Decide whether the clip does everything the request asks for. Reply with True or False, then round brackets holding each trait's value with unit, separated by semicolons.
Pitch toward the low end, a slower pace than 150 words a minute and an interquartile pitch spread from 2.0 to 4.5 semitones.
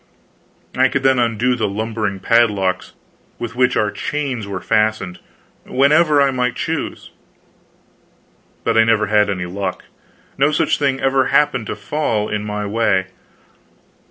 True (115 Hz; 140 wpm; 4.1 semitones)